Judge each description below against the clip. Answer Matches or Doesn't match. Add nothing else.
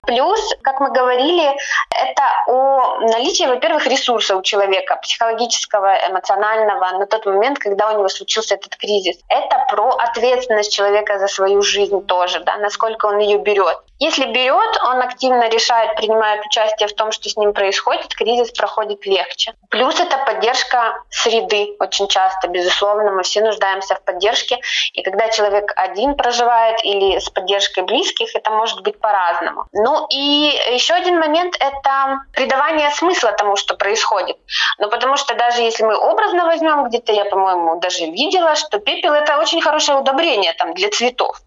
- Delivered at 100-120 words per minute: Doesn't match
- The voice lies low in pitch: Doesn't match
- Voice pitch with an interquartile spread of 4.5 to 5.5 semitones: Matches